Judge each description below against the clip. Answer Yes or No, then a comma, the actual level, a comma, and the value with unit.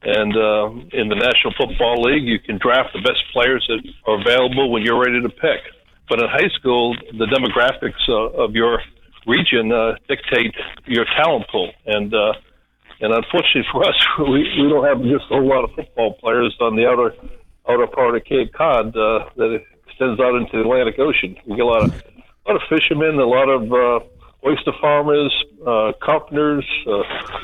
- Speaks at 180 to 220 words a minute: Yes, average, 190 wpm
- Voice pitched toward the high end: No, low, 125 Hz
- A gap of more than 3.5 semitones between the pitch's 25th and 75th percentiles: Yes, average, 4.5 semitones